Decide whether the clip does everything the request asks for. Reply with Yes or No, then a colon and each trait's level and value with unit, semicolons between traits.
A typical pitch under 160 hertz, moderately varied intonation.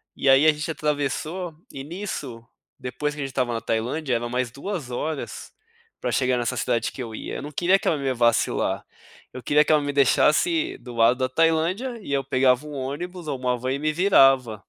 Yes: medium, 140 Hz; average, 3.8 semitones